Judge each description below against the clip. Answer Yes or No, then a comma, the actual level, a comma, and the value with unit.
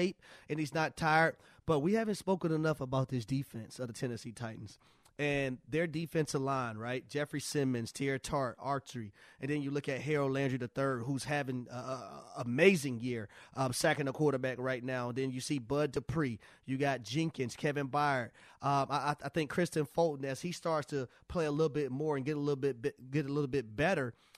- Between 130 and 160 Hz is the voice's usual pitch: Yes, medium, 140 Hz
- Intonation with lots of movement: No, average, 3.0 semitones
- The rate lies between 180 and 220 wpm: Yes, average, 200 wpm